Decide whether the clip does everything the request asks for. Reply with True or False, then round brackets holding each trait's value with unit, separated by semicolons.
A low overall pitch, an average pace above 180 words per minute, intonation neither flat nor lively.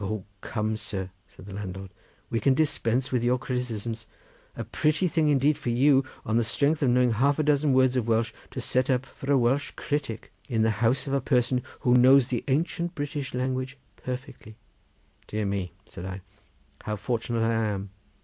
True (125 Hz; 190 wpm; 3.6 semitones)